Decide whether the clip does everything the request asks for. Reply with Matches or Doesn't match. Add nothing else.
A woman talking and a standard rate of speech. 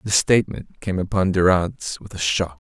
Doesn't match